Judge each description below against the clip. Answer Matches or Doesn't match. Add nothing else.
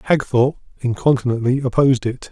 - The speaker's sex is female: Doesn't match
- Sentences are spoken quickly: Doesn't match